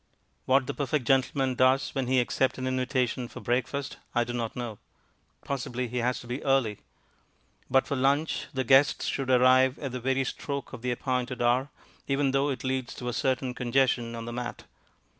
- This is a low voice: Yes, low, 130 Hz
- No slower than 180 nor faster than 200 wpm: Yes, average, 190 wpm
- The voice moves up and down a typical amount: No, narrow, 1.6 semitones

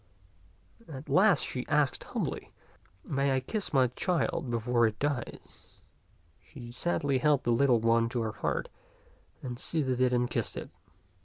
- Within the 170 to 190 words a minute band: No, average, 160 wpm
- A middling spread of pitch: Yes, average, 3.3 semitones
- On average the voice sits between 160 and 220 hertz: No, low, 130 Hz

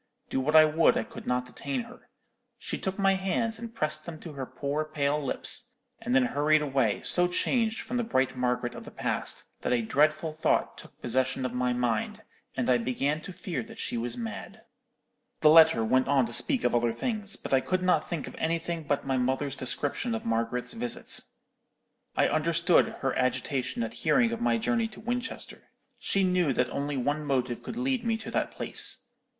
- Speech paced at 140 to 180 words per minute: No, average, 200 wpm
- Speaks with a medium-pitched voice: Yes, medium, 150 Hz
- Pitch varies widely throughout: Yes, wide, 7.3 semitones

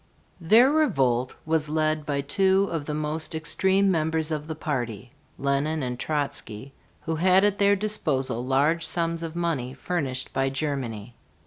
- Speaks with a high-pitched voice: No, medium, 155 Hz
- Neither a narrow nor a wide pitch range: Yes, average, 4.0 semitones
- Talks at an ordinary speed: Yes, average, 150 wpm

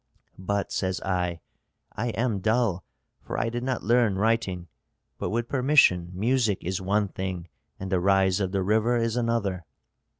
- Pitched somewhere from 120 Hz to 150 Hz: No, low, 100 Hz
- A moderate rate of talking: Yes, average, 160 wpm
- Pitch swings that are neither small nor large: Yes, average, 3.8 semitones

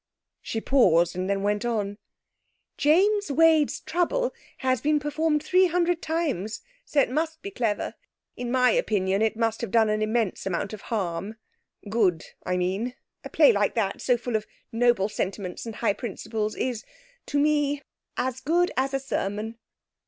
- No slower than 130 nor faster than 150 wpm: No, average, 165 wpm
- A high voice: Yes, high, 240 Hz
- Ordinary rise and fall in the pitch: No, wide, 6.1 semitones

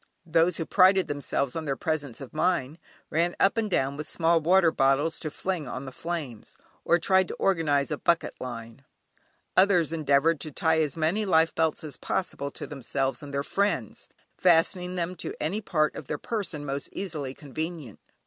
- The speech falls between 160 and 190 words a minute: Yes, average, 180 wpm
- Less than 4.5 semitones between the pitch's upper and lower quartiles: Yes, average, 3.7 semitones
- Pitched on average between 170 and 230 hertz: No, medium, 160 Hz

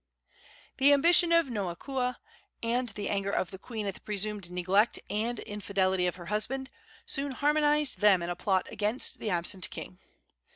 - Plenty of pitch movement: Yes, wide, 5.7 semitones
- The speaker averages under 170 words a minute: Yes, average, 160 wpm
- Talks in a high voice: Yes, high, 210 Hz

